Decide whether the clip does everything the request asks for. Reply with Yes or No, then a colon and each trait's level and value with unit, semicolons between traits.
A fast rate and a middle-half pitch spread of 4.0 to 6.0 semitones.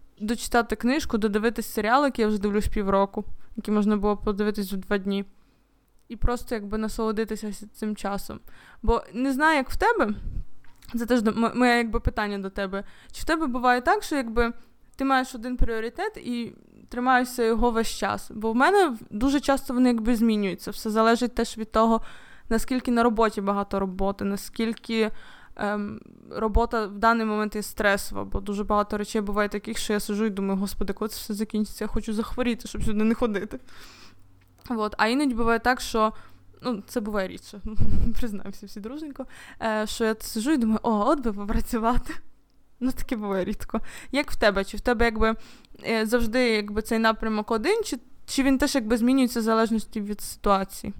No: fast, 175 wpm; narrow, 2.5 semitones